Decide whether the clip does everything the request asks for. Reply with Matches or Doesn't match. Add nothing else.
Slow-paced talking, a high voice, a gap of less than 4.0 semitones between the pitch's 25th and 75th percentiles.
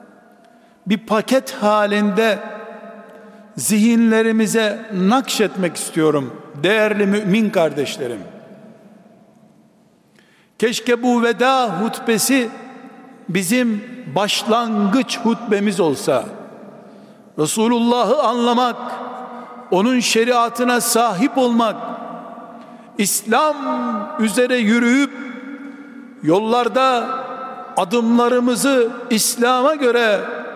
Matches